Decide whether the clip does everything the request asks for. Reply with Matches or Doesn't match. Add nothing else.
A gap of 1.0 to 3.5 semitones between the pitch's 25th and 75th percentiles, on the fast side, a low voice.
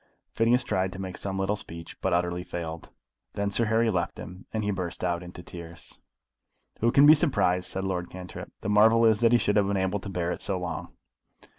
Matches